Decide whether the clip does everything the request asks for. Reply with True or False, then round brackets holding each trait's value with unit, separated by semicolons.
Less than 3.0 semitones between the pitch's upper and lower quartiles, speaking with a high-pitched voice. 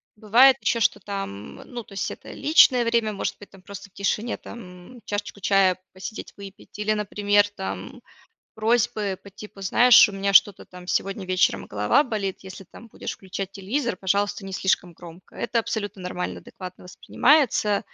True (2.6 semitones; 200 Hz)